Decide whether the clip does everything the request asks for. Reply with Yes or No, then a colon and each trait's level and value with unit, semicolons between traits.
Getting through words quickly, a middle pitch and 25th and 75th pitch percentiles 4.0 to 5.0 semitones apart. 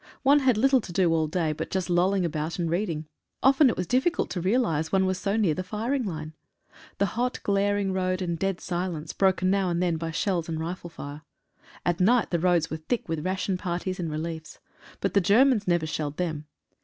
No: fast, 215 wpm; medium, 180 Hz; average, 3.5 semitones